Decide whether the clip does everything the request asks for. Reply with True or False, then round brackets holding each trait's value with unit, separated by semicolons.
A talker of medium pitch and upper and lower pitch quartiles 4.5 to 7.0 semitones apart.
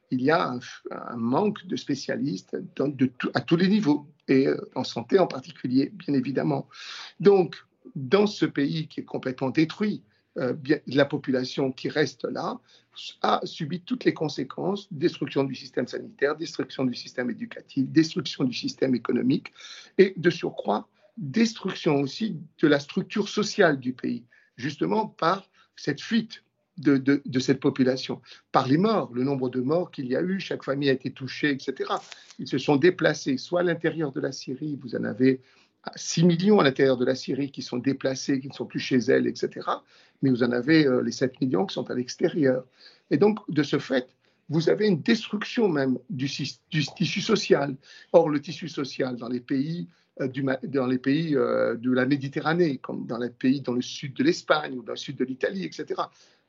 True (145 Hz; 5.3 semitones)